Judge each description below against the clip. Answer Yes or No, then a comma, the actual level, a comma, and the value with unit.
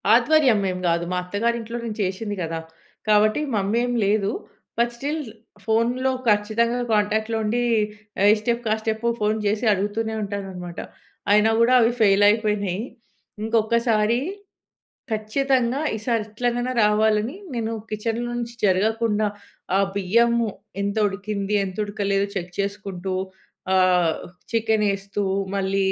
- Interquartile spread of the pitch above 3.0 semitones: No, narrow, 2.6 semitones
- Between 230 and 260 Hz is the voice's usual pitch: No, high, 215 Hz